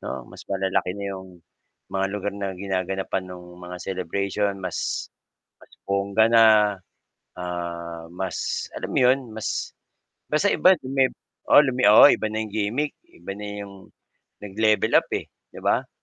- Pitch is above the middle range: No, low, 100 Hz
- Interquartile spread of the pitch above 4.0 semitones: No, average, 2.9 semitones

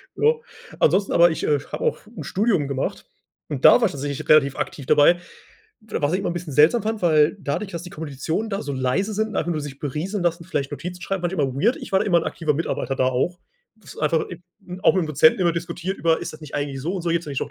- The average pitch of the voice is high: No, medium, 165 Hz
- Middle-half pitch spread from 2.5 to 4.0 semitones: No, average, 4.6 semitones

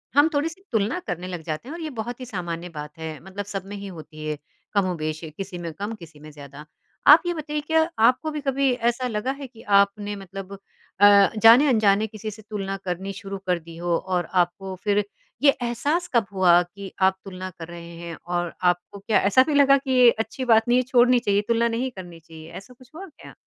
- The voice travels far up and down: Yes, wide, 6.0 semitones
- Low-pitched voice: No, high, 200 Hz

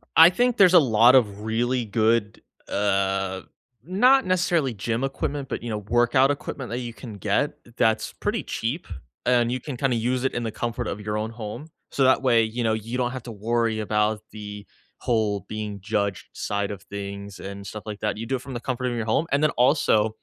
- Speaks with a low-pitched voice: Yes, low, 115 Hz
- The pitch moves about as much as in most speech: Yes, average, 3.5 semitones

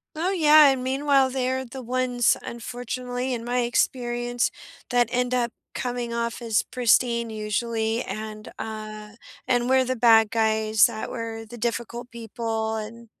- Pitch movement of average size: No, narrow, 2.1 semitones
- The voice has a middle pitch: No, high, 240 Hz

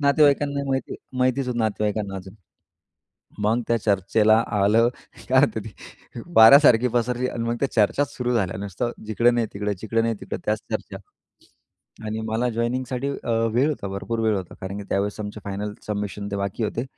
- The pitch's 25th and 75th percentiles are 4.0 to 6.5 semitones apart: No, average, 3.3 semitones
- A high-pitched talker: No, low, 110 Hz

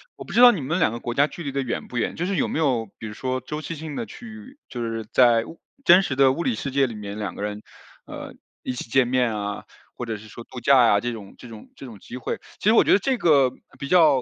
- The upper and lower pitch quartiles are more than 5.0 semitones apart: Yes, wide, 5.4 semitones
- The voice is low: Yes, low, 130 Hz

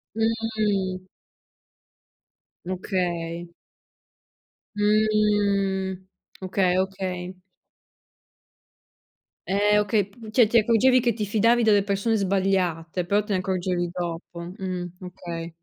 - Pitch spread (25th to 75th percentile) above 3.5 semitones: No, average, 2.8 semitones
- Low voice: No, high, 195 Hz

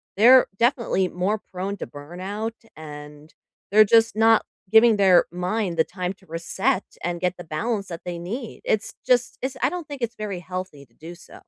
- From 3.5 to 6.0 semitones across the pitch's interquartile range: Yes, average, 4.3 semitones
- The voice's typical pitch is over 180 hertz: Yes, high, 190 Hz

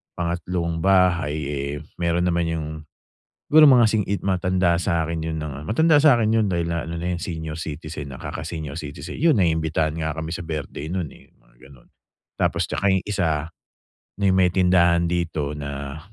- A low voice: Yes, very low, 85 Hz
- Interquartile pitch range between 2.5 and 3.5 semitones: Yes, average, 2.9 semitones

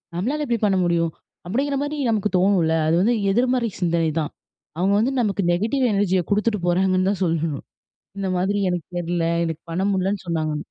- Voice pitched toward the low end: No, high, 190 Hz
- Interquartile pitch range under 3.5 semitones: No, average, 3.8 semitones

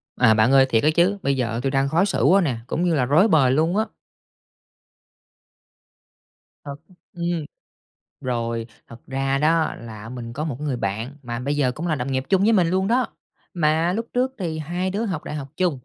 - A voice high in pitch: No, medium, 150 Hz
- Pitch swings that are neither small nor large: No, wide, 5.7 semitones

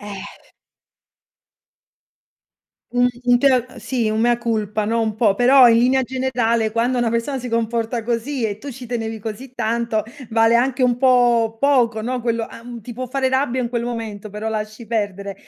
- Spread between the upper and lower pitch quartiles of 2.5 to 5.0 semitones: No, narrow, 2.0 semitones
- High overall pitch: Yes, high, 235 Hz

